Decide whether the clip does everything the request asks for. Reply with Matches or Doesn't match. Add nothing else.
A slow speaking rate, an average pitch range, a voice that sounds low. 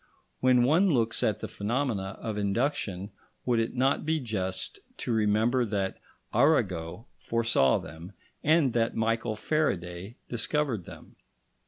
Matches